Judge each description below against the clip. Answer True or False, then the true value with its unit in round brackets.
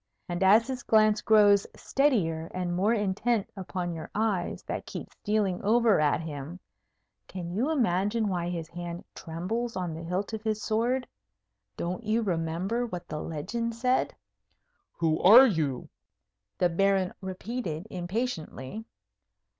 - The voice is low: False (190 Hz)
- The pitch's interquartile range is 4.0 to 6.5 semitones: True (4.5 semitones)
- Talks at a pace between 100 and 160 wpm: True (140 wpm)